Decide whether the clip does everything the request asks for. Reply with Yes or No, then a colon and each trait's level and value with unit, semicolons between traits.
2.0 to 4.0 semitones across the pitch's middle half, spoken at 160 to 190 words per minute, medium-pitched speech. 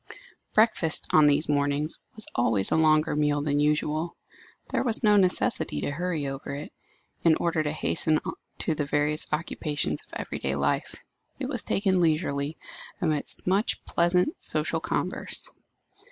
No: average, 2.9 semitones; average, 150 wpm; medium, 155 Hz